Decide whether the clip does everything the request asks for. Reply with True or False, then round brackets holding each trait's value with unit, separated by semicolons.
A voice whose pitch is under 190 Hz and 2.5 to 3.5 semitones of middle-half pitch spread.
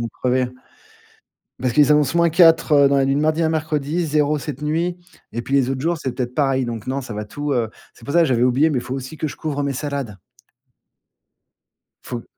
True (140 Hz; 3.2 semitones)